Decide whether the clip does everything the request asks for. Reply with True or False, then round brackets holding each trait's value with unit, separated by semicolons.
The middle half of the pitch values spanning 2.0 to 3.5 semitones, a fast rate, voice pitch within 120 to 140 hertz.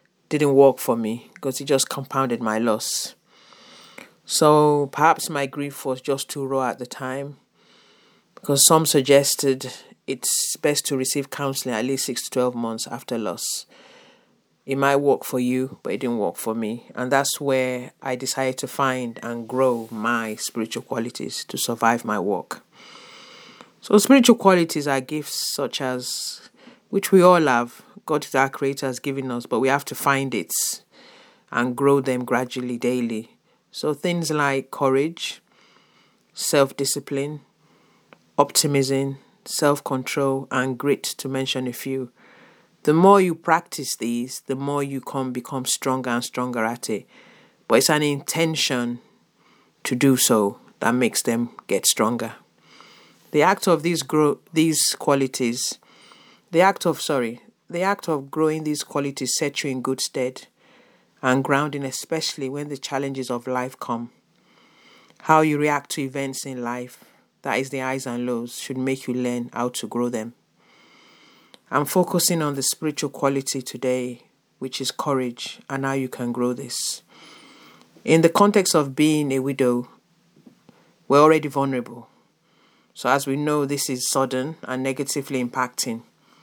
False (2.6 semitones; 155 wpm; 135 Hz)